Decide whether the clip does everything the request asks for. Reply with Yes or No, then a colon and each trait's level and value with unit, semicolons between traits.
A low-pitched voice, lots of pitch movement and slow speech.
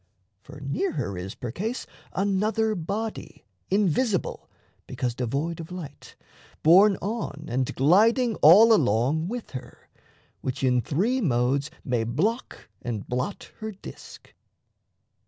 No: medium, 160 Hz; wide, 8.7 semitones; slow, 120 wpm